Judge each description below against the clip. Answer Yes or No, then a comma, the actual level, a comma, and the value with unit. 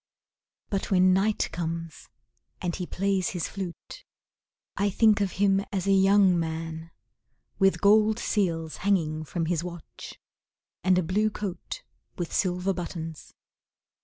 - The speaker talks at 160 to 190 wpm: No, slow, 135 wpm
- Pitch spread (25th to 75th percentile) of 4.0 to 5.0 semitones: No, average, 2.9 semitones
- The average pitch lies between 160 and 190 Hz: Yes, medium, 185 Hz